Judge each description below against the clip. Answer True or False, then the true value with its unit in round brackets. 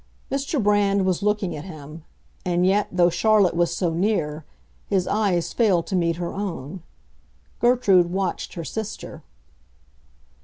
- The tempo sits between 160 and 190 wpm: False (140 wpm)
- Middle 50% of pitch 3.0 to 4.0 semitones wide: True (3.3 semitones)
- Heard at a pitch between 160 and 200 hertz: True (185 Hz)